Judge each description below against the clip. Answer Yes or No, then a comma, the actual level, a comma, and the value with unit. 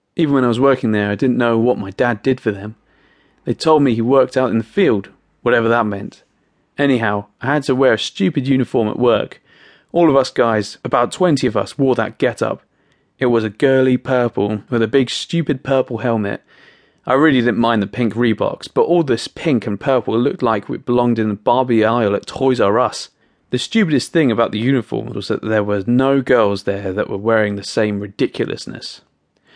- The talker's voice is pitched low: Yes, low, 120 Hz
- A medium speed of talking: No, fast, 210 wpm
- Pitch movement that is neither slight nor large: Yes, average, 3.5 semitones